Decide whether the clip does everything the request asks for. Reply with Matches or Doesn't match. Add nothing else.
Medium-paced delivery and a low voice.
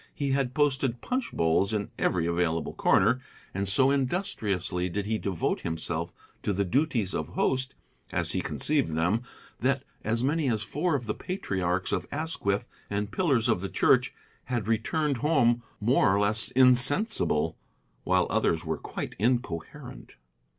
Matches